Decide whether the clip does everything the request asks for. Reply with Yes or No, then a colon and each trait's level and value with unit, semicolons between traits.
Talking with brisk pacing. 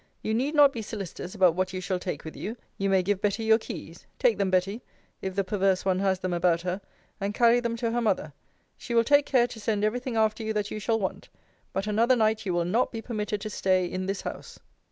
Yes: fast, 250 wpm